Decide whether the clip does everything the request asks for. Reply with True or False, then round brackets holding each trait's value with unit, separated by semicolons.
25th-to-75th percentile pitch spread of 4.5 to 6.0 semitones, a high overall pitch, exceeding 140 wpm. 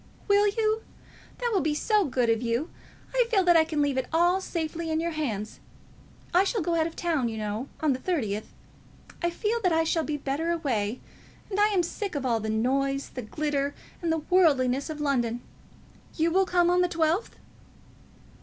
True (5.2 semitones; 315 Hz; 200 wpm)